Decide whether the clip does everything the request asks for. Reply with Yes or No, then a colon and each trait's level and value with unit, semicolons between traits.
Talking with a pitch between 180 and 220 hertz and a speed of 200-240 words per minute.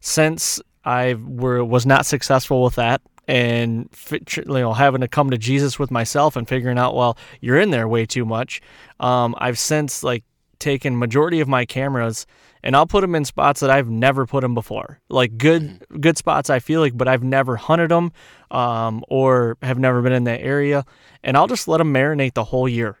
No: low, 130 Hz; fast, 205 wpm